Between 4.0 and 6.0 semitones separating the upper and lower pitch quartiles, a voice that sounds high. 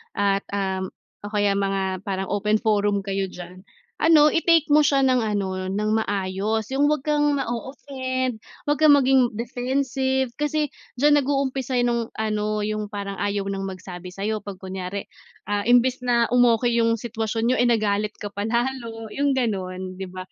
Yes: average, 4.7 semitones; high, 220 Hz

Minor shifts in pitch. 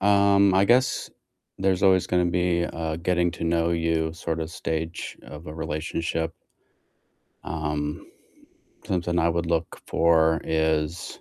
Yes: narrow, 1.9 semitones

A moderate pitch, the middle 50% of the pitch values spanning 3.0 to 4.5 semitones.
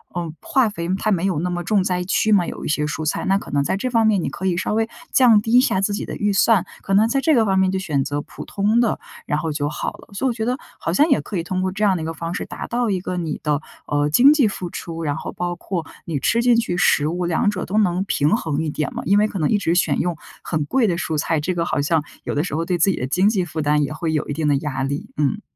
No: medium, 180 Hz; average, 5.1 semitones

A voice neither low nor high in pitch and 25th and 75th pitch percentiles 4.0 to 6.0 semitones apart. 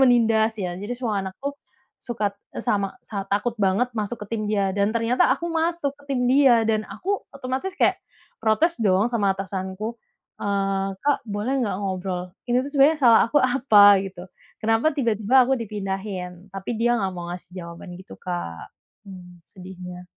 No: high, 210 Hz; average, 4.3 semitones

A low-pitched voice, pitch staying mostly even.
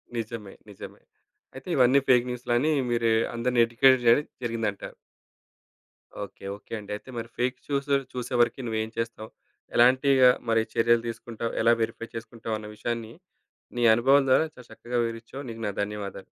Yes: low, 115 Hz; narrow, 2.0 semitones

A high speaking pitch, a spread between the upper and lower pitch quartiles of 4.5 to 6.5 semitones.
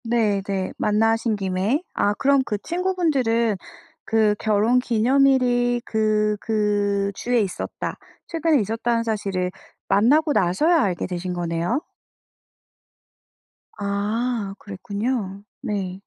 No: high, 215 Hz; average, 3.5 semitones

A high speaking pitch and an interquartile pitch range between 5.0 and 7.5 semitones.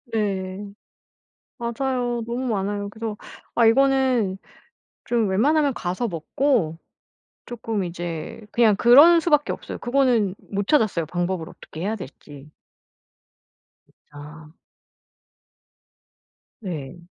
Yes: high, 210 Hz; wide, 5.4 semitones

